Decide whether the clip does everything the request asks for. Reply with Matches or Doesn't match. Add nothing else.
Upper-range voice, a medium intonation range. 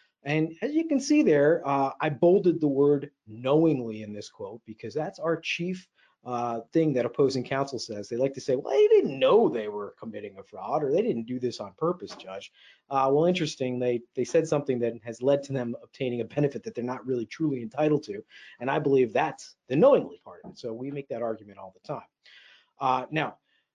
Doesn't match